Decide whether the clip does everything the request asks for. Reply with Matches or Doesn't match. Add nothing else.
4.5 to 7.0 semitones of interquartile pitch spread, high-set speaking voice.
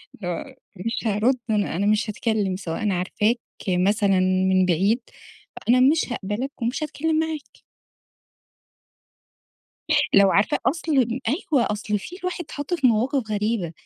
Matches